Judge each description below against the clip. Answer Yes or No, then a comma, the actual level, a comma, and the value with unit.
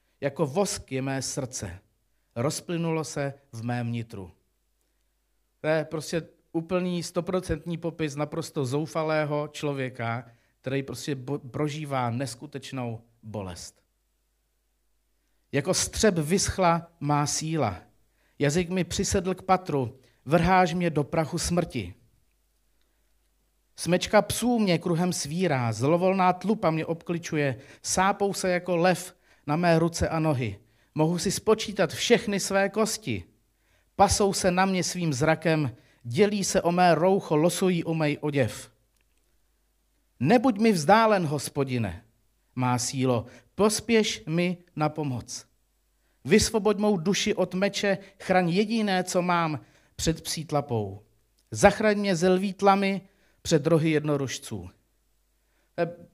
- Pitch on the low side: No, medium, 155 Hz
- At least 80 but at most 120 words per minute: Yes, slow, 115 wpm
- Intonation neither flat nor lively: No, wide, 6.8 semitones